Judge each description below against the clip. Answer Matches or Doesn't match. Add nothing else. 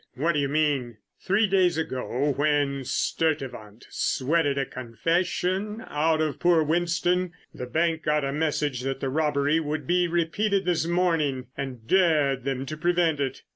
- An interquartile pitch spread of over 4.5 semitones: Doesn't match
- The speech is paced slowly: Doesn't match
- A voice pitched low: Doesn't match